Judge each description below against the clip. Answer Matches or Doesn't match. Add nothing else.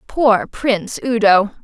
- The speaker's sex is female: Matches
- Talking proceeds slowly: Matches